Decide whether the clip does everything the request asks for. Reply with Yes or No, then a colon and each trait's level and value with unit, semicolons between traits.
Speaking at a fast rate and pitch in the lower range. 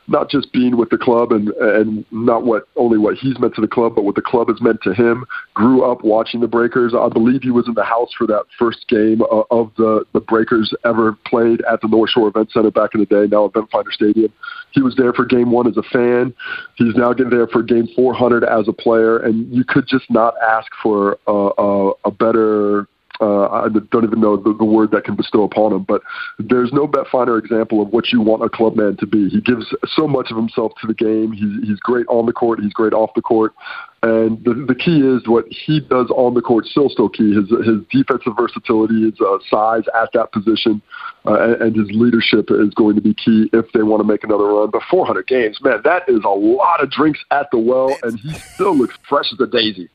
Yes: fast, 240 wpm; low, 115 Hz